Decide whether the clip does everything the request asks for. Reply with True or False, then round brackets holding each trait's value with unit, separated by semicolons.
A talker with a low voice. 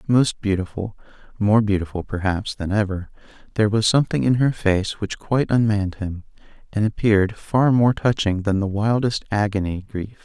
True (105 Hz)